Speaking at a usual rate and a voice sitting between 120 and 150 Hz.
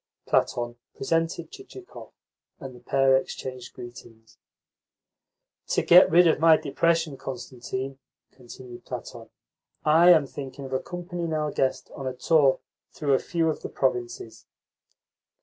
No: slow, 130 wpm; low, 135 Hz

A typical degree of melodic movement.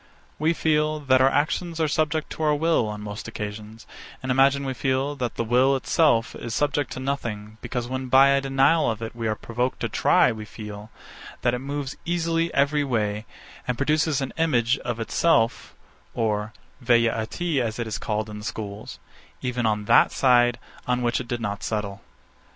Yes: average, 4.2 semitones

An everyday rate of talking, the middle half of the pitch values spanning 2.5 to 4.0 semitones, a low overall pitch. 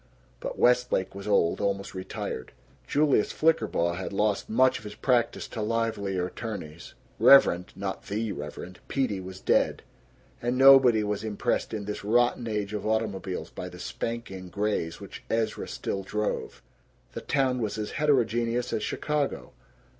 Yes: average, 145 wpm; average, 3.7 semitones; low, 105 Hz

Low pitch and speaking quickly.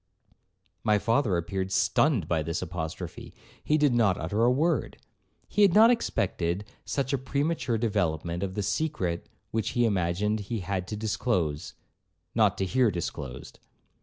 No: low, 105 Hz; average, 150 wpm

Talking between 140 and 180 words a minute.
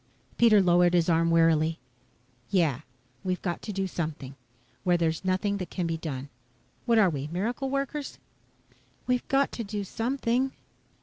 Yes: average, 150 wpm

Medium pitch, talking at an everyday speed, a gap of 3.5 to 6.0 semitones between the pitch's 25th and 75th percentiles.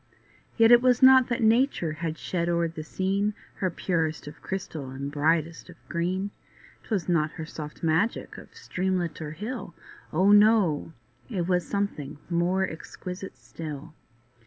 Yes: medium, 175 Hz; average, 145 wpm; average, 4.3 semitones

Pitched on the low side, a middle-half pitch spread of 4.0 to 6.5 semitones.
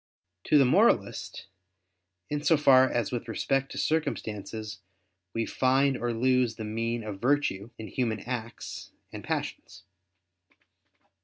No: low, 120 Hz; average, 3.4 semitones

